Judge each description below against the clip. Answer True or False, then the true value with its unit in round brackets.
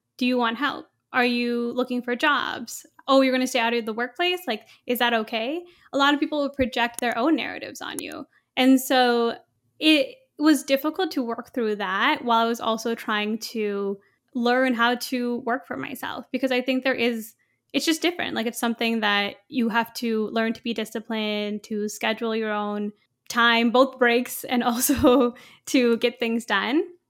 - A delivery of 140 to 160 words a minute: False (190 wpm)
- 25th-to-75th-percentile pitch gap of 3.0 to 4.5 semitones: False (2.6 semitones)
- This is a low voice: False (240 Hz)